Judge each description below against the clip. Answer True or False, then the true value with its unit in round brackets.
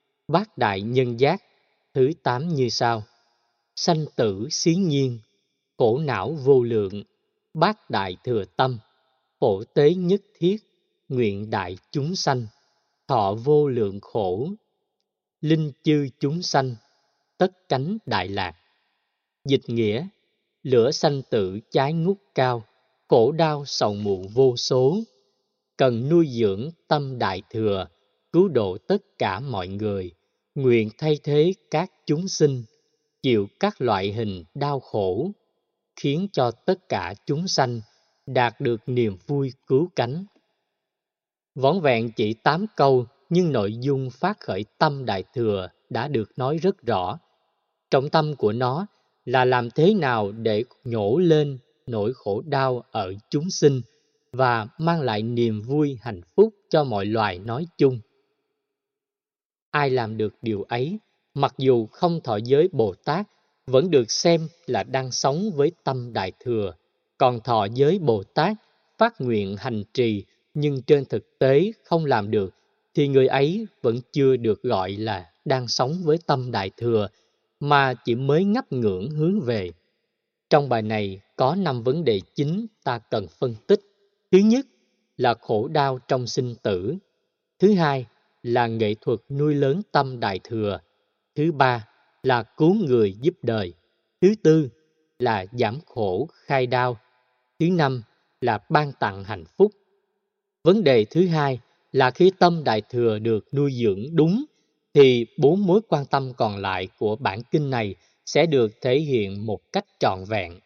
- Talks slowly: True (150 wpm)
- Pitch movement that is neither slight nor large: False (6.3 semitones)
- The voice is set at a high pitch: False (135 Hz)